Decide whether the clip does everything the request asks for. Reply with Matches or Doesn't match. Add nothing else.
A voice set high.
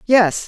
Matches